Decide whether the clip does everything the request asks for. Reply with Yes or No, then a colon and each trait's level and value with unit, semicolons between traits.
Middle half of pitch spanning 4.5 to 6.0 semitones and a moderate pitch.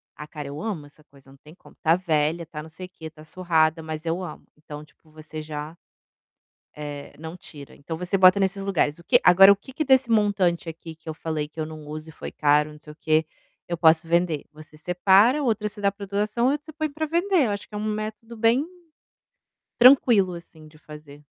Yes: average, 4.9 semitones; medium, 170 Hz